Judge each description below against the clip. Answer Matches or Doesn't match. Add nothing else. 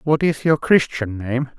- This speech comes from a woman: Doesn't match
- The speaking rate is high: Doesn't match